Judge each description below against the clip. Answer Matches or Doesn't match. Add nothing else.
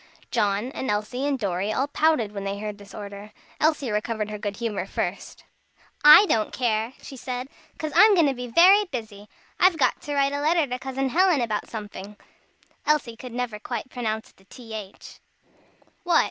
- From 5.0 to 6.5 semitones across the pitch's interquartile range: Matches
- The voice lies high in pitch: Matches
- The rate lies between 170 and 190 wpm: Matches